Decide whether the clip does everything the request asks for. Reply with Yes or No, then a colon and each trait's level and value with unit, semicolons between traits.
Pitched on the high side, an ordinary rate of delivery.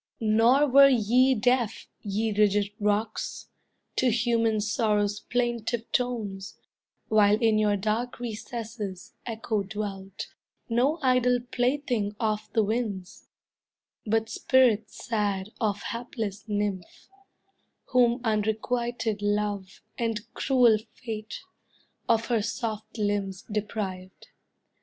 No: high, 220 Hz; slow, 100 wpm